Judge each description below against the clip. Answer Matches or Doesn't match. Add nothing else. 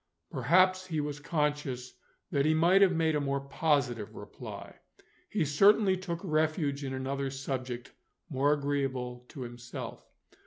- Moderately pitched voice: Matches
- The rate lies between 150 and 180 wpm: Doesn't match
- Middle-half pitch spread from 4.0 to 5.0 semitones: Doesn't match